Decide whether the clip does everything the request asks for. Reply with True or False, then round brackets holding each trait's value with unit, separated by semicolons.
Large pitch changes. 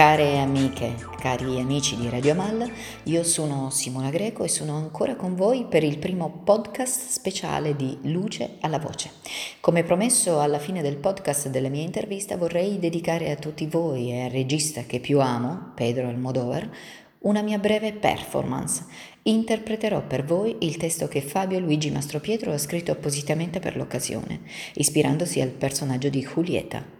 True (5.7 semitones)